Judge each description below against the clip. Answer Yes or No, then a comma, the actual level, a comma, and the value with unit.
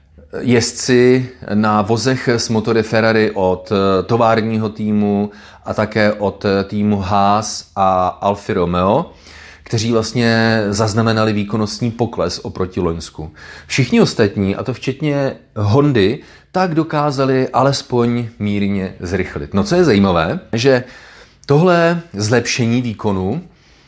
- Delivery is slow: Yes, slow, 110 wpm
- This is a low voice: Yes, low, 110 Hz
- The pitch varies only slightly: No, average, 3.4 semitones